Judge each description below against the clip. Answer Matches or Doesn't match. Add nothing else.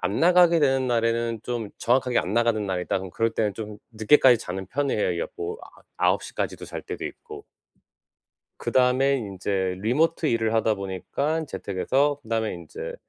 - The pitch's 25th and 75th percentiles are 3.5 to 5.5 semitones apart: Matches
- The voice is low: Matches